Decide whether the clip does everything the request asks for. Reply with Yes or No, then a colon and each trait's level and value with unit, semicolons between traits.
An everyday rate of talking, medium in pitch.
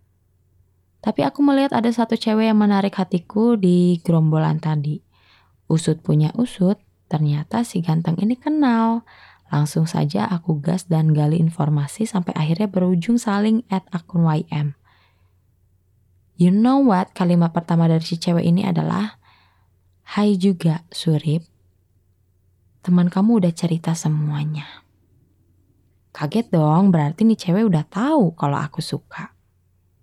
Yes: average, 125 wpm; medium, 165 Hz